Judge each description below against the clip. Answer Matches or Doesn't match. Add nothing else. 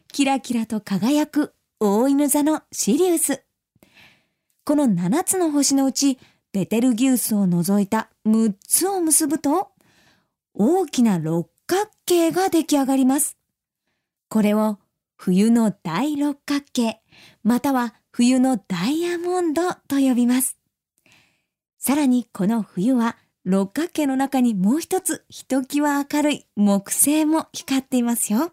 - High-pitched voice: Matches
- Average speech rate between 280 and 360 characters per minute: Doesn't match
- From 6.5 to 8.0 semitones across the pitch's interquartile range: Doesn't match